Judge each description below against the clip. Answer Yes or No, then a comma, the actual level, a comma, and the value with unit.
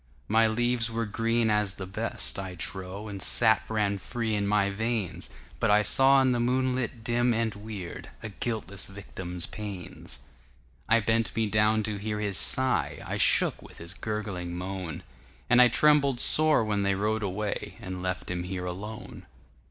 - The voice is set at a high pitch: No, low, 105 Hz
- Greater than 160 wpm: No, average, 150 wpm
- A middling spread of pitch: Yes, average, 3.3 semitones